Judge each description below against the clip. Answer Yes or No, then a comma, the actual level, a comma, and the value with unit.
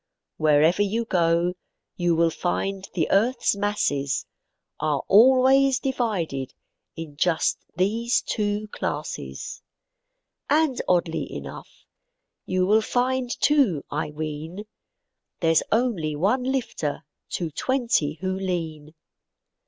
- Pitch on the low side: No, medium, 185 Hz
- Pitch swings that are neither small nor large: No, wide, 6.6 semitones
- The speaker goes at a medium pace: No, slow, 105 wpm